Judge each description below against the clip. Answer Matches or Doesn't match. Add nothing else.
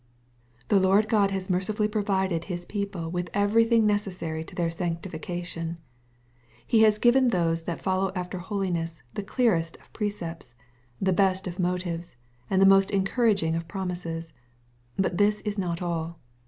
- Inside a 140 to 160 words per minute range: Matches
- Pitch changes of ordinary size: Matches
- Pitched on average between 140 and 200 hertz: Matches